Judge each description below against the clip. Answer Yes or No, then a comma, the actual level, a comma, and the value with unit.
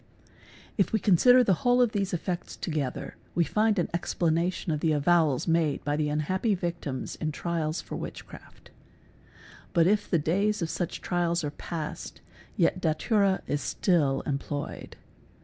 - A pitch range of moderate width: Yes, average, 3.5 semitones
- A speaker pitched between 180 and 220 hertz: No, medium, 170 Hz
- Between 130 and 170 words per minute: Yes, average, 165 wpm